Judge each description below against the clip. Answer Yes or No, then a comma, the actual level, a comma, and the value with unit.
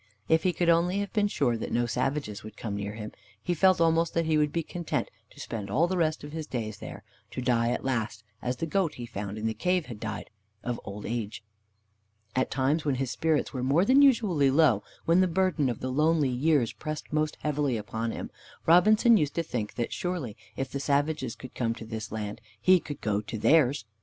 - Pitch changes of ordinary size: No, wide, 6.3 semitones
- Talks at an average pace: No, fast, 220 wpm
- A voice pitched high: No, medium, 140 Hz